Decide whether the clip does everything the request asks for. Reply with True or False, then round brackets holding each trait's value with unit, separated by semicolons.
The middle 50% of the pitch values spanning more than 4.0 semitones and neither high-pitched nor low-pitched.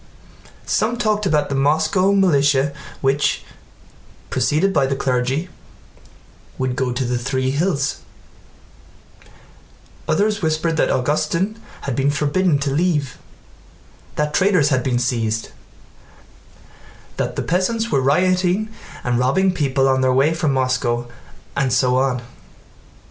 True (5.6 semitones; 145 Hz)